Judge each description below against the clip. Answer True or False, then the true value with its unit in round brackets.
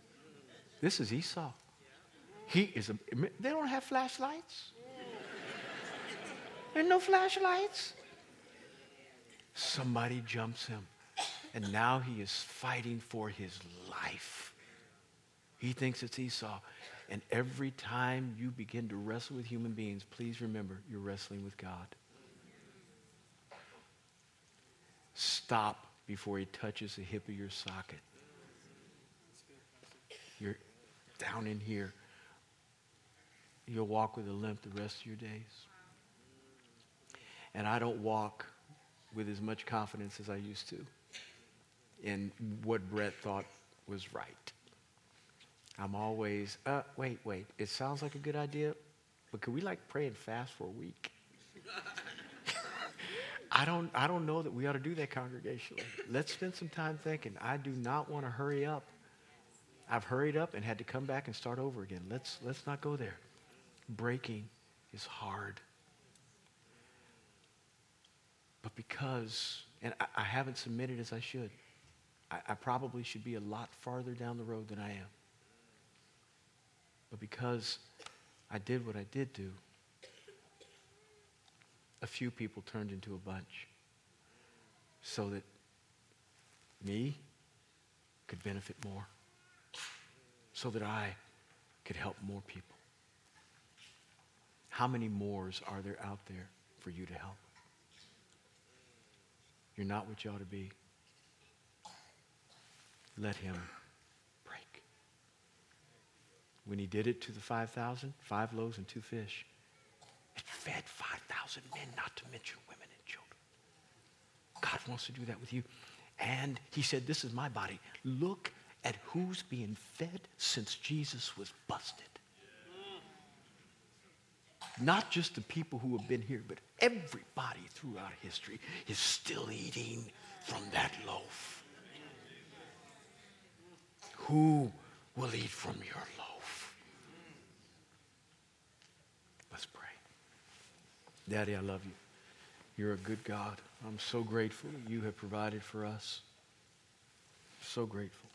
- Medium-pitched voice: False (115 Hz)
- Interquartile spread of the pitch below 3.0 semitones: False (4.2 semitones)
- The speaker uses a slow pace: True (125 wpm)